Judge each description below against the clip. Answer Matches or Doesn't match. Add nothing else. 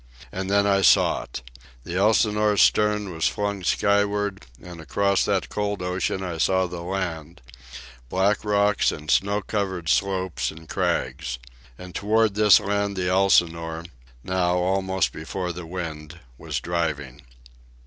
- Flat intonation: Doesn't match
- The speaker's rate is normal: Doesn't match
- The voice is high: Doesn't match